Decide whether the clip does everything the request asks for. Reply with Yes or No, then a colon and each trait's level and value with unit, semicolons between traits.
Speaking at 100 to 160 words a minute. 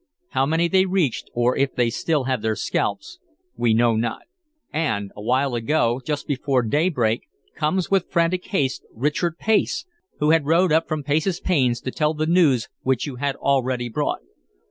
No: average, 170 wpm